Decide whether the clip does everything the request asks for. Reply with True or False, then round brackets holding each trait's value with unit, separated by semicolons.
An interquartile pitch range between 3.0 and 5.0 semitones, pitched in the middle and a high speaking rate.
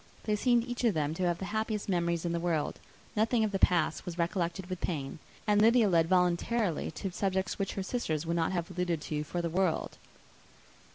True (3.6 semitones; 180 Hz; 210 wpm)